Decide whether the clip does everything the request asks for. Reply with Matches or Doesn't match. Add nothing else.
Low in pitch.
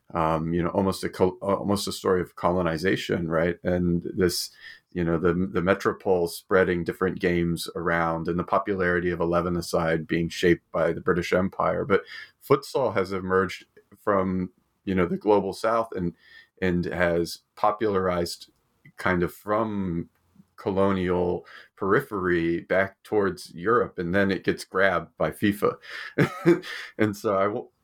Matches